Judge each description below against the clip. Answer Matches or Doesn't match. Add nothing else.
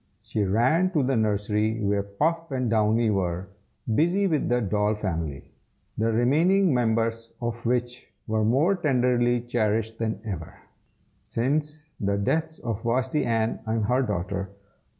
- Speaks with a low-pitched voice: Matches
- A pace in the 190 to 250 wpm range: Doesn't match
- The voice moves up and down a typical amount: Matches